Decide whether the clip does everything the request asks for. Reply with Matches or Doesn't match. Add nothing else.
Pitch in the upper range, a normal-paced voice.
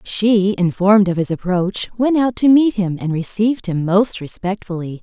Matches